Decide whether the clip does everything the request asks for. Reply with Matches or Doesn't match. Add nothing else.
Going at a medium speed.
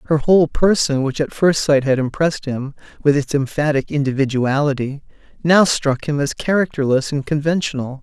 Matches